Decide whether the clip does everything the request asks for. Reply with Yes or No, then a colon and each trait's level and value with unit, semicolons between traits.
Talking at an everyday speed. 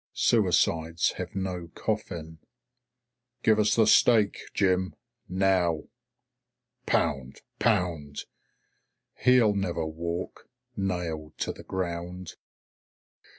No: slow, 85 wpm